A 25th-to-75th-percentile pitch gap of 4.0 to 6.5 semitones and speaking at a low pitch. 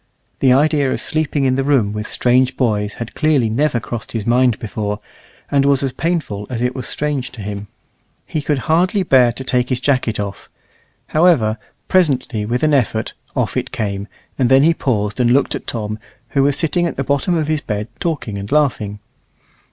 Yes: average, 5.0 semitones; low, 130 Hz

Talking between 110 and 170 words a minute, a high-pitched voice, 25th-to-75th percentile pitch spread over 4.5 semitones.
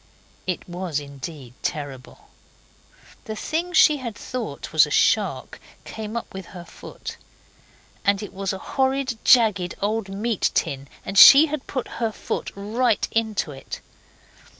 Yes: average, 140 wpm; high, 210 Hz; average, 5.2 semitones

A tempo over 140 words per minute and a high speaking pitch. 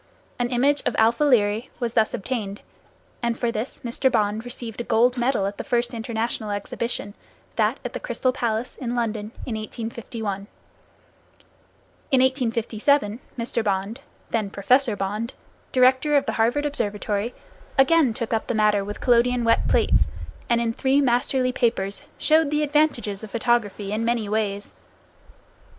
Yes: average, 155 wpm; high, 235 Hz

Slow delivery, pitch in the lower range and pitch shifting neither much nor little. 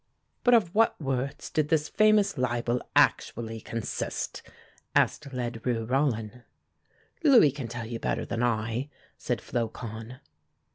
Yes: slow, 125 wpm; low, 125 Hz; average, 4.5 semitones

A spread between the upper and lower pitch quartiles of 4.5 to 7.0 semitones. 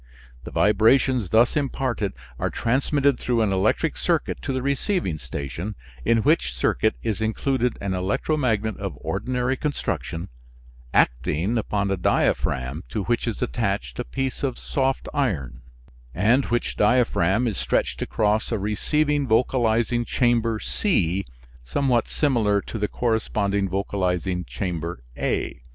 Yes: average, 5.1 semitones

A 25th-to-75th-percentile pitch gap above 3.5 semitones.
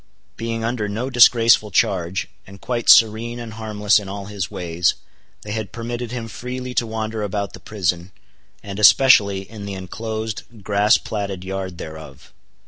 No: average, 2.7 semitones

